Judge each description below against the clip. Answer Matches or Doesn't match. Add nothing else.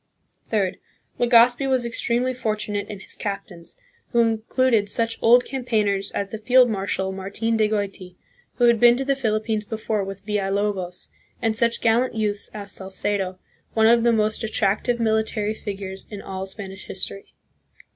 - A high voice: Matches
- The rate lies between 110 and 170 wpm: Matches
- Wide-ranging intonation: Doesn't match